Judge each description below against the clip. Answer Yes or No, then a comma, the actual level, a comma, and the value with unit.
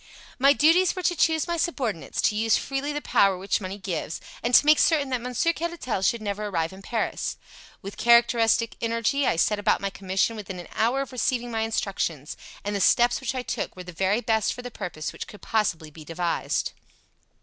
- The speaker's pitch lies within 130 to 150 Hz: No, high, 225 Hz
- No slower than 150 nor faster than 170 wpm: No, fast, 205 wpm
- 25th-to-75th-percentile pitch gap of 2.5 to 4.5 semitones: No, average, 5.1 semitones